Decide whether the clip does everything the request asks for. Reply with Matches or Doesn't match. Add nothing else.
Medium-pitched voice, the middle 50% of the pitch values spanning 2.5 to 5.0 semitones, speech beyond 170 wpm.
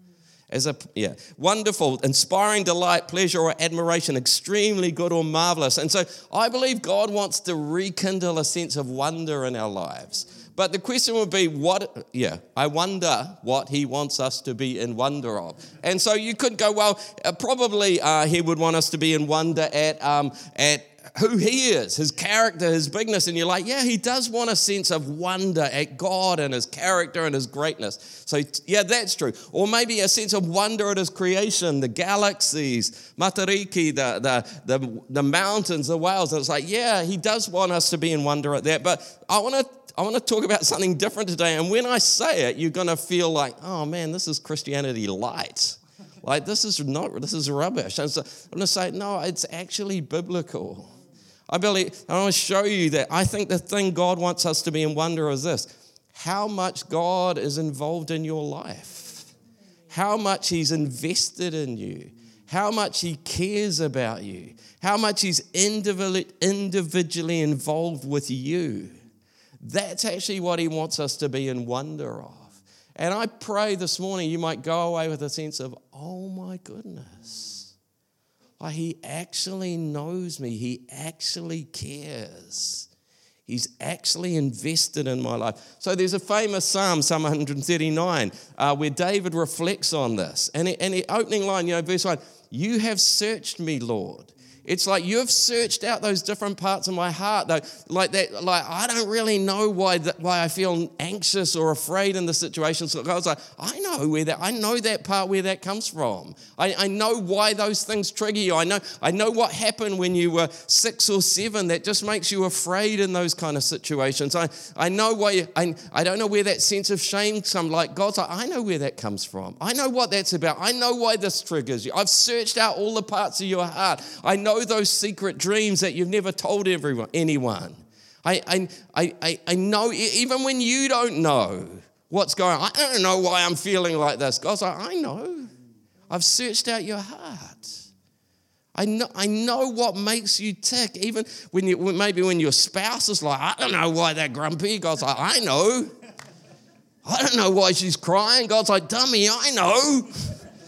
Matches